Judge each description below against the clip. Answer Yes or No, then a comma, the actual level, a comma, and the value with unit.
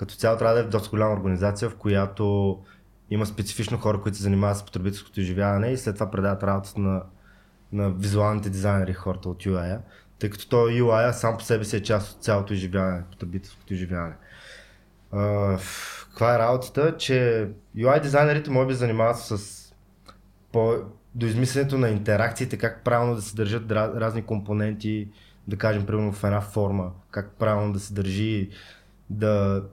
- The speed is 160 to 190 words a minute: Yes, fast, 165 wpm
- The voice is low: Yes, low, 105 Hz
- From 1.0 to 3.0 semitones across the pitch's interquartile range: Yes, narrow, 2.4 semitones